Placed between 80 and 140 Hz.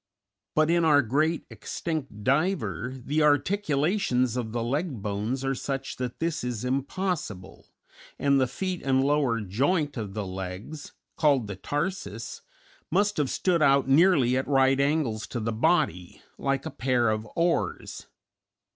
Yes: low, 135 Hz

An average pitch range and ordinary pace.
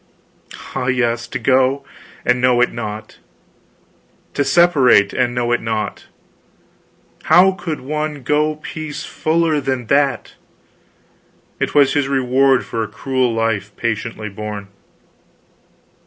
No: average, 3.8 semitones; slow, 120 wpm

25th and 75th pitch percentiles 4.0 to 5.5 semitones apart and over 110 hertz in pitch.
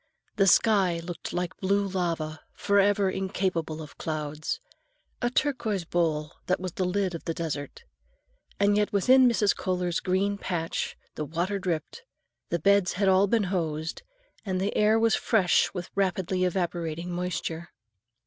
No: average, 3.2 semitones; medium, 185 Hz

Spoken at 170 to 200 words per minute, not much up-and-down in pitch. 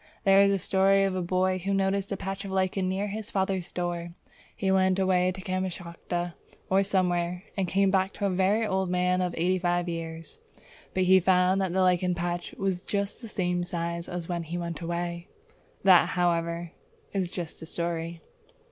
Yes: average, 185 wpm; narrow, 1.7 semitones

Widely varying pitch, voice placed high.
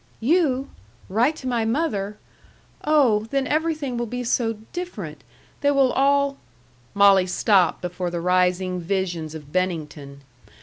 Yes: wide, 7.3 semitones; high, 210 Hz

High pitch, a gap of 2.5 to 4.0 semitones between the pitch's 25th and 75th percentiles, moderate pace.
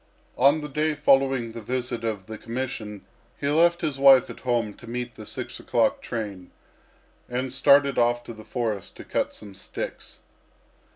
No: low, 120 Hz; average, 3.6 semitones; average, 170 wpm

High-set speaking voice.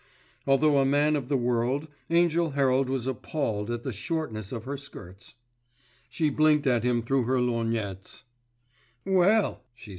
No: low, 135 Hz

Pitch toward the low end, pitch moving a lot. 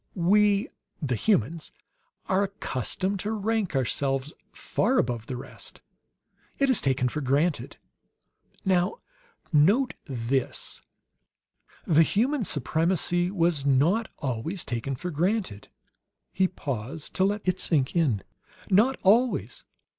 No: medium, 170 Hz; wide, 6.8 semitones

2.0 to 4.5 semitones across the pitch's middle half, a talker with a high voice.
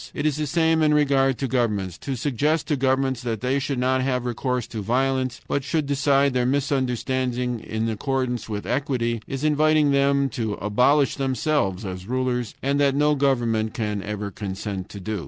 No: average, 3.6 semitones; low, 130 Hz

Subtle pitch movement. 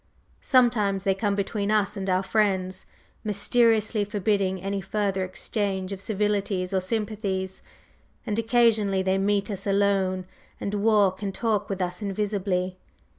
Yes: narrow, 1.8 semitones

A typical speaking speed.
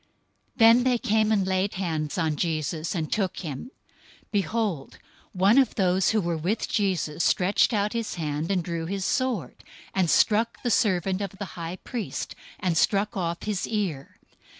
Yes: average, 170 wpm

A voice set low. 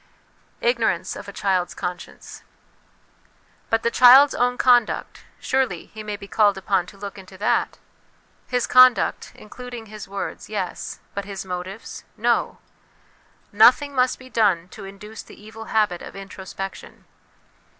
No: high, 210 Hz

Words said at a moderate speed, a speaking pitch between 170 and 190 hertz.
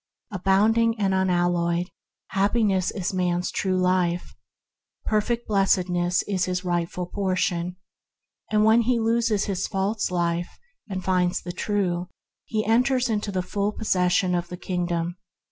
No: slow, 130 wpm; medium, 185 Hz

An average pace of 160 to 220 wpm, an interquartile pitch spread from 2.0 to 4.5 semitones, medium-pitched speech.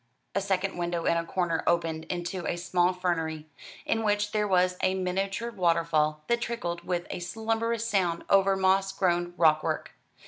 Yes: average, 170 wpm; narrow, 2.4 semitones; medium, 180 Hz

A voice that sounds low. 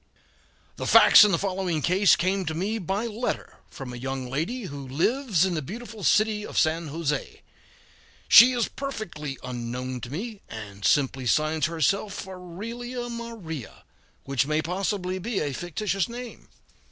No: medium, 180 Hz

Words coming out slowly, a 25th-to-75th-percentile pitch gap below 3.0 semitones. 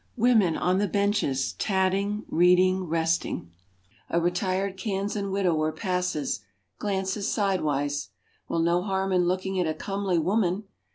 Yes: slow, 125 wpm; narrow, 2.6 semitones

